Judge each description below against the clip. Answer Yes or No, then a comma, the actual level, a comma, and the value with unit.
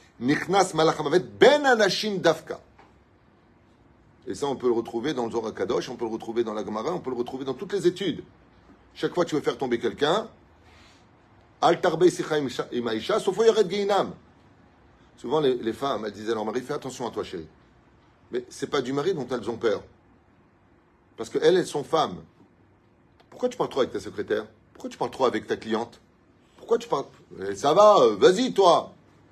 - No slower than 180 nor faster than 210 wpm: Yes, average, 185 wpm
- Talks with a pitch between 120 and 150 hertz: No, medium, 160 Hz